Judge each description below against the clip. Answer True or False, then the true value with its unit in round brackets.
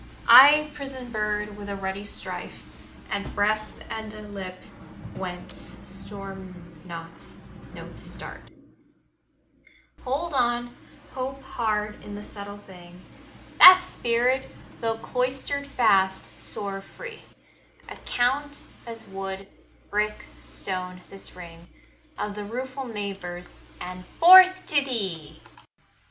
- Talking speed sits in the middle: False (110 wpm)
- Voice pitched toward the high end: True (210 Hz)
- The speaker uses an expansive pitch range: False (5.0 semitones)